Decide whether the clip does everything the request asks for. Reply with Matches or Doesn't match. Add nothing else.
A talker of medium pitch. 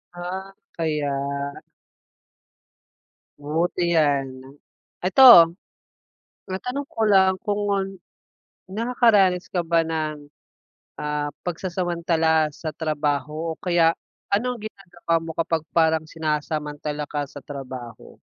Matches